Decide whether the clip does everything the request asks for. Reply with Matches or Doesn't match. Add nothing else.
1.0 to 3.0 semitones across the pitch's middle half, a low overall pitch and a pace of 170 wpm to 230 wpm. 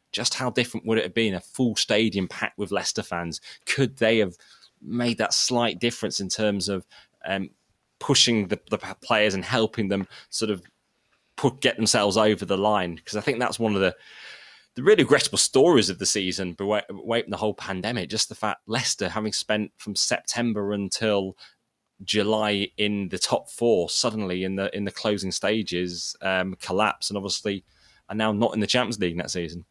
Matches